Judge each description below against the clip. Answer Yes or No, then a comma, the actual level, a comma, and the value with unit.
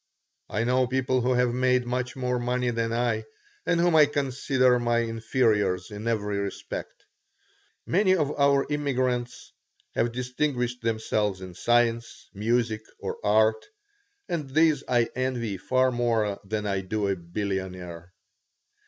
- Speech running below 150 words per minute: Yes, slow, 135 wpm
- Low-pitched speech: Yes, low, 120 Hz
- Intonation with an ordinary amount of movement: Yes, average, 3.1 semitones